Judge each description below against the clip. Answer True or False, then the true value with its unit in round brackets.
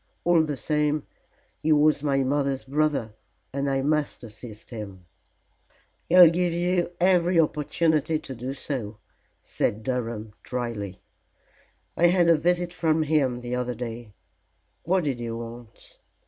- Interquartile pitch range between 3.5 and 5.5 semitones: True (5.1 semitones)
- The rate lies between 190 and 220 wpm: False (135 wpm)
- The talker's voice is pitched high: False (140 Hz)